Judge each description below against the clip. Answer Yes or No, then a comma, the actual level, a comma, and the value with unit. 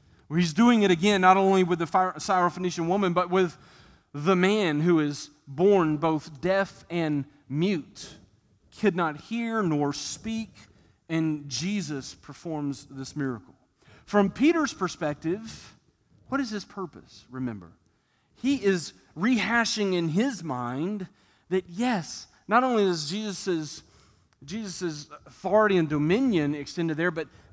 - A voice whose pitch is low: No, medium, 175 Hz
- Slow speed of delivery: Yes, slow, 125 wpm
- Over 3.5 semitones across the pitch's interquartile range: Yes, average, 5.1 semitones